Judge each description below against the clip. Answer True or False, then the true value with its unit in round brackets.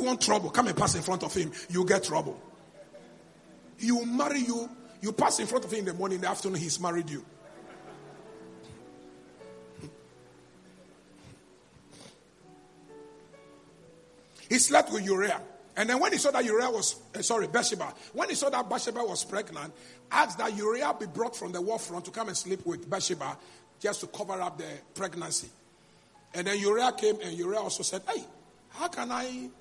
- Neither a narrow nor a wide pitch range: False (6.1 semitones)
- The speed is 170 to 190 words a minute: True (175 wpm)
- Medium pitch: False (195 Hz)